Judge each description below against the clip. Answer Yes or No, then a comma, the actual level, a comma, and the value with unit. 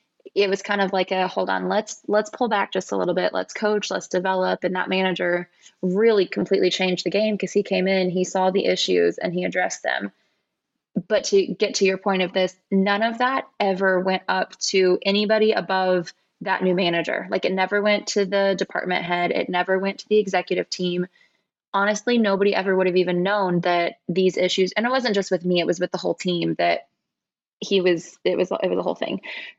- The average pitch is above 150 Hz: Yes, high, 190 Hz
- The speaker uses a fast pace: Yes, fast, 215 wpm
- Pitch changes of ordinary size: No, narrow, 2.1 semitones